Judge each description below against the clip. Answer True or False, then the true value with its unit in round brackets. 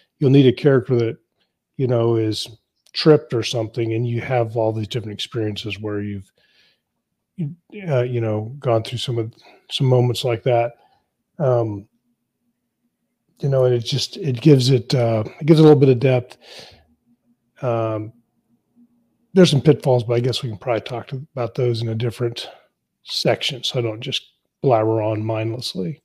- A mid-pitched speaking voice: False (120 Hz)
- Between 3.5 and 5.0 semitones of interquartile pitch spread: False (3.0 semitones)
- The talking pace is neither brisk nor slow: True (175 wpm)